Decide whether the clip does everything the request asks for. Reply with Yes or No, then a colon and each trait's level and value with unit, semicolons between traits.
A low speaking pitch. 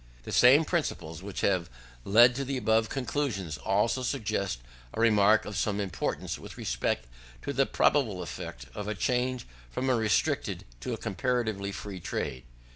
Yes: low, 110 Hz